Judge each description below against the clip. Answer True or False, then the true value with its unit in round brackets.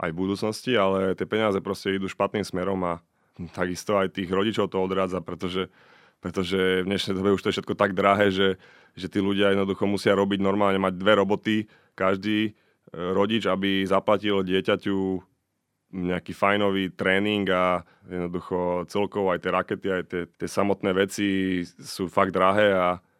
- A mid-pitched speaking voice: False (95 Hz)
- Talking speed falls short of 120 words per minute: False (160 wpm)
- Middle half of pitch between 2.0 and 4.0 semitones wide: False (1.3 semitones)